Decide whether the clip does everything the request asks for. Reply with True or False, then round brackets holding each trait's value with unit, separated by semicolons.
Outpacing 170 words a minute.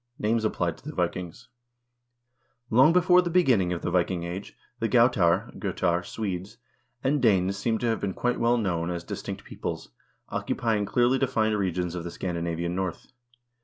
False (165 wpm)